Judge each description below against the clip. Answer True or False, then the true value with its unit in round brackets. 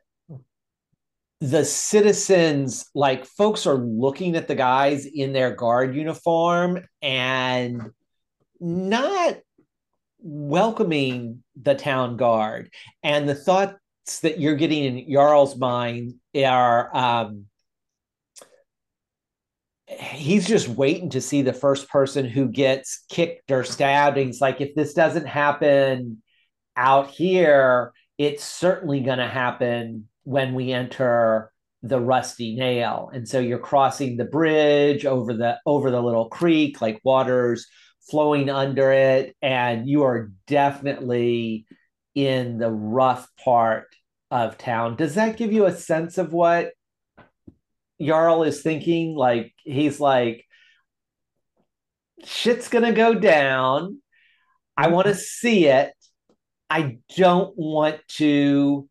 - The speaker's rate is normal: False (120 wpm)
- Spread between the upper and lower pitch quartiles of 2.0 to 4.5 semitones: True (4.2 semitones)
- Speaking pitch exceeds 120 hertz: True (140 Hz)